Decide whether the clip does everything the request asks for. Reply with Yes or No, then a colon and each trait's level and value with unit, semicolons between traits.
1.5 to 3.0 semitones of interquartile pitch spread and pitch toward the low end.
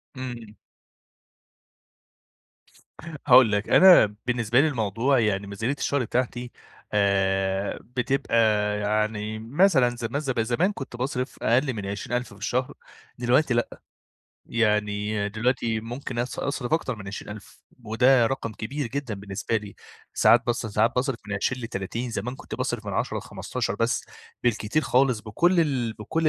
No: average, 3.5 semitones; low, 120 Hz